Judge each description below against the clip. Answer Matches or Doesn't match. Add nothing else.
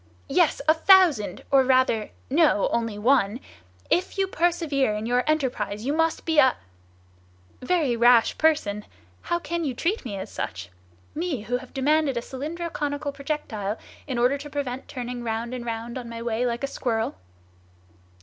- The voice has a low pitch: Doesn't match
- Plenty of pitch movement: Doesn't match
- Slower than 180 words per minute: Matches